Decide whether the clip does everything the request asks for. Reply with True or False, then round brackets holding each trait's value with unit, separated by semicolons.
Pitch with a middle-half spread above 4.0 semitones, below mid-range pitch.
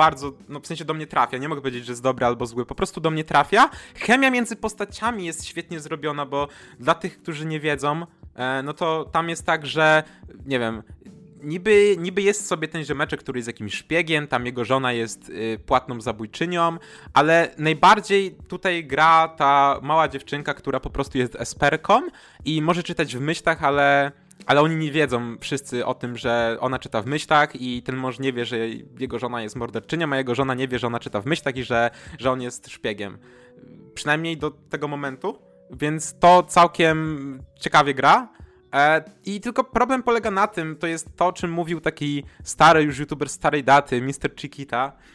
False (4.4 semitones; 150 Hz)